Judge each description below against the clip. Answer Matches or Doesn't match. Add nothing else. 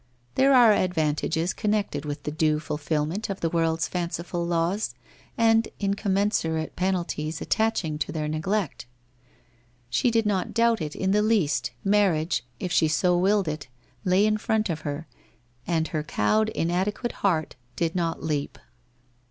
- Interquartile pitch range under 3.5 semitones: Doesn't match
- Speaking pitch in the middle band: Matches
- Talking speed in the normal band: Matches